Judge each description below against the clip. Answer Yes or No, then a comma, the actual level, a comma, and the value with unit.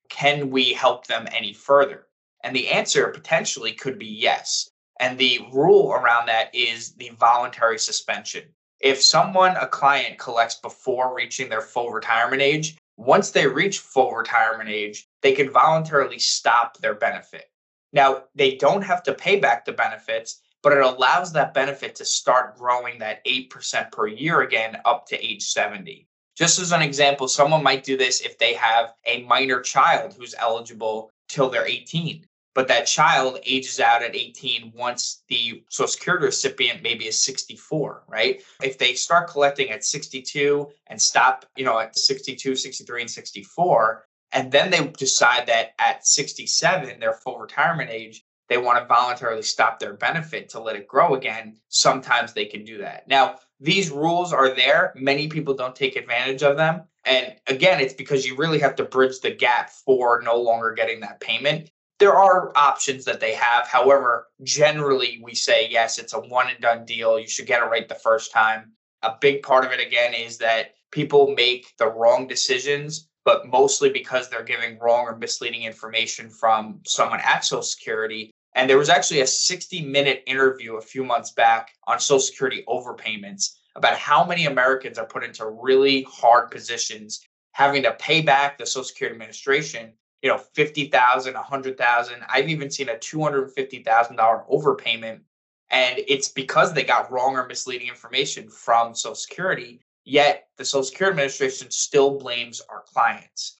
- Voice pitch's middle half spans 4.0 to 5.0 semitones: Yes, average, 4.3 semitones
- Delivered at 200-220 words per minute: No, average, 175 wpm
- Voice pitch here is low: Yes, low, 130 Hz